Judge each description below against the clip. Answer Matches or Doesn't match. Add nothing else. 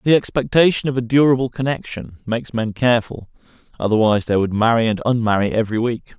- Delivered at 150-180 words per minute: Matches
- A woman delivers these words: Doesn't match